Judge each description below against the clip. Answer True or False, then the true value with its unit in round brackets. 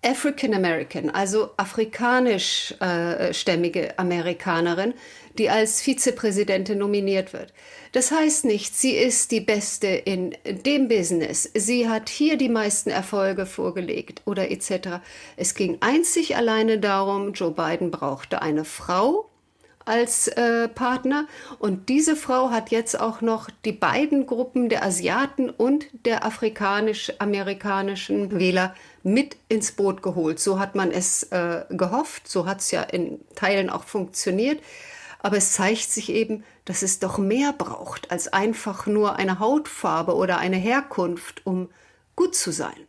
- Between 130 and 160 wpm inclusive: True (140 wpm)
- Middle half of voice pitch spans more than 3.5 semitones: True (4.5 semitones)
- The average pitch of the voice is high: True (210 Hz)